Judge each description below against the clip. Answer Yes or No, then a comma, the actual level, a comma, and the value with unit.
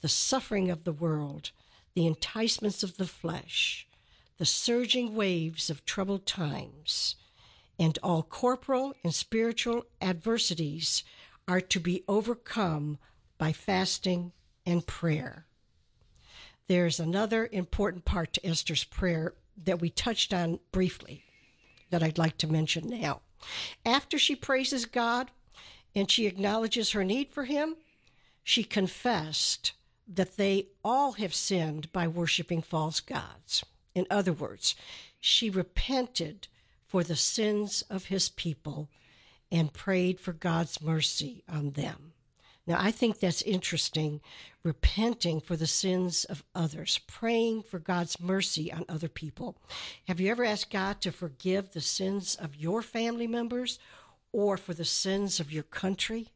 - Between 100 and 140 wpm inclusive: Yes, slow, 135 wpm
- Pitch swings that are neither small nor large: Yes, average, 4.8 semitones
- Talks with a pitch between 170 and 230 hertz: Yes, medium, 185 Hz